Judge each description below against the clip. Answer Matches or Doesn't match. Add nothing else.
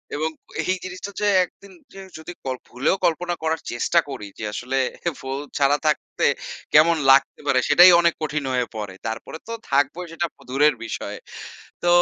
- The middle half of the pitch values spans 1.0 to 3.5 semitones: Doesn't match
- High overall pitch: Doesn't match